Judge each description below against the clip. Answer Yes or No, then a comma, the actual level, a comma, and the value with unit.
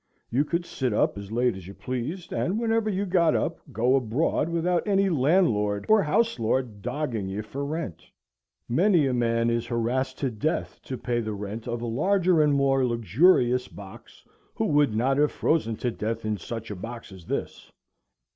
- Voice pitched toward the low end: Yes, low, 125 Hz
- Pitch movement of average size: No, wide, 6.1 semitones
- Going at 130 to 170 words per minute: No, average, 185 wpm